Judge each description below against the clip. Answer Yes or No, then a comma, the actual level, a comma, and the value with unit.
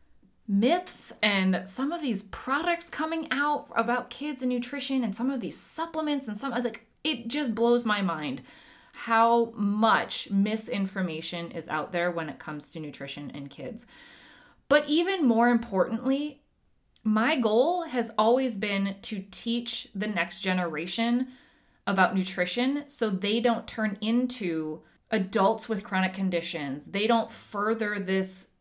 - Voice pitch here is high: Yes, high, 225 Hz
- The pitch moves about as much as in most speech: Yes, average, 5.0 semitones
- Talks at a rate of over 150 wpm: No, average, 140 wpm